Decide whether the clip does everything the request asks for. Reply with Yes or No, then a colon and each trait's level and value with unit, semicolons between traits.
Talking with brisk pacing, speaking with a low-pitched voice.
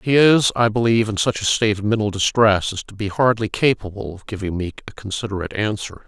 Yes: fast, 215 wpm; low, 105 Hz